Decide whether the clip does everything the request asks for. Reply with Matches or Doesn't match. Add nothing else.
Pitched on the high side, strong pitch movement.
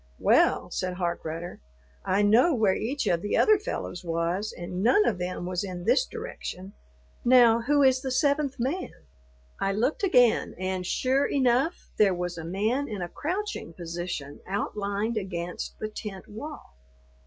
Matches